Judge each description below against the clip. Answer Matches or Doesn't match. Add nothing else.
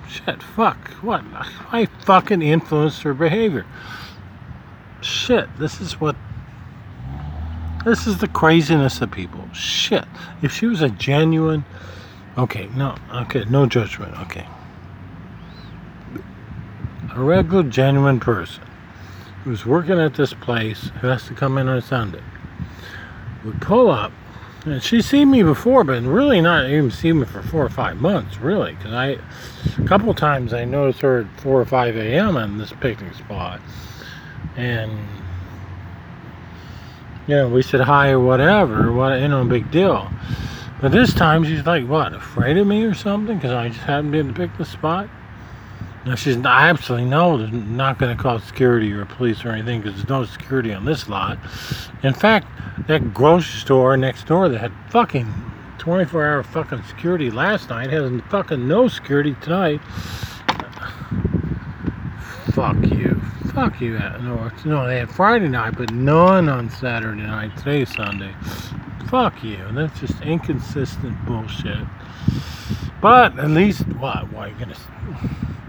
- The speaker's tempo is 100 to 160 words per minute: Matches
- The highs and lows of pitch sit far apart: Matches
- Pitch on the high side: Doesn't match